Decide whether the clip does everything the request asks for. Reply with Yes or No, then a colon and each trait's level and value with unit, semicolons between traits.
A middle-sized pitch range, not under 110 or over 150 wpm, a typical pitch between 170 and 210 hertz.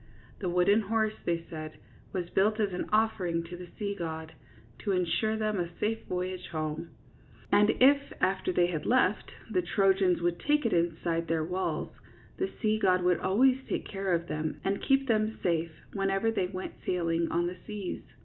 No: average, 3.8 semitones; average, 180 wpm; medium, 185 Hz